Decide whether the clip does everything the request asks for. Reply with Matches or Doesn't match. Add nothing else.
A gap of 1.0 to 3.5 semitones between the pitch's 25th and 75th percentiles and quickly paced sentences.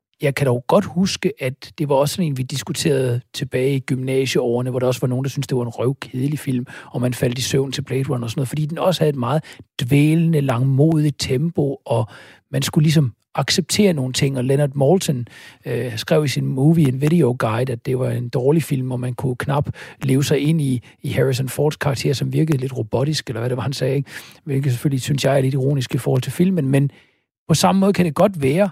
Matches